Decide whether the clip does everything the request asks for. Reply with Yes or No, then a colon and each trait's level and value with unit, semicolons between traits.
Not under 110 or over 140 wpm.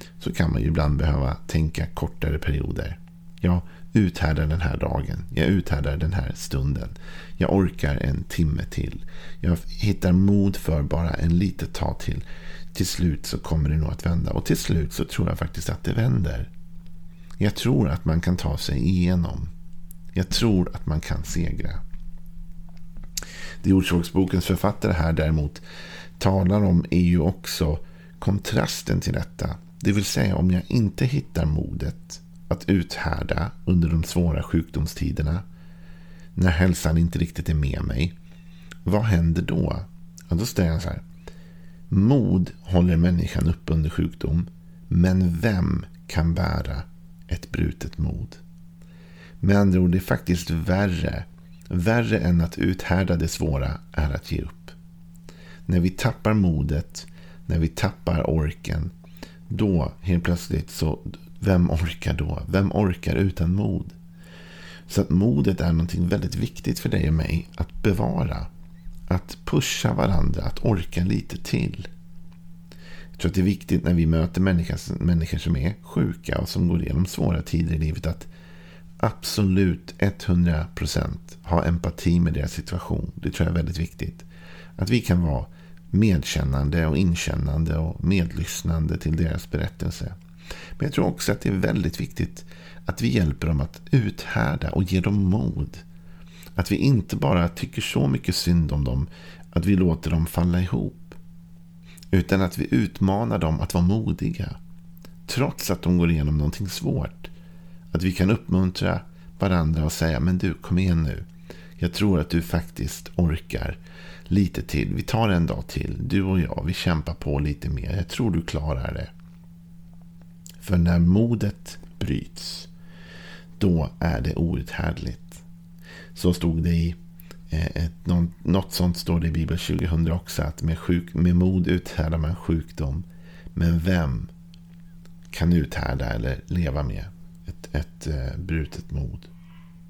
No: average, 150 wpm